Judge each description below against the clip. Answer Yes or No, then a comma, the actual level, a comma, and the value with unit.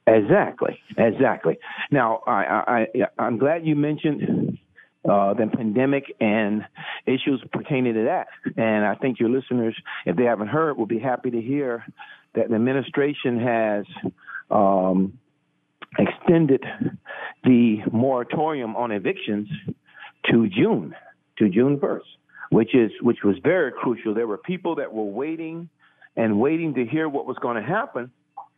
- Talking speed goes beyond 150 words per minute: No, average, 145 wpm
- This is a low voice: Yes, low, 125 Hz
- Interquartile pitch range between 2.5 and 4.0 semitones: No, average, 4.8 semitones